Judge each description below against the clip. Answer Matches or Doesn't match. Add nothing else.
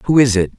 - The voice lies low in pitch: Matches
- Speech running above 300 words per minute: Matches